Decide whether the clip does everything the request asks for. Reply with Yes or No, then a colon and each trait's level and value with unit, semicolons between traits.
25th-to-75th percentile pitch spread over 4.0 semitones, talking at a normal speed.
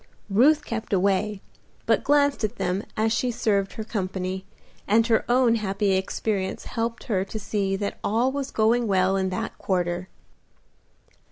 No: average, 3.2 semitones; average, 155 wpm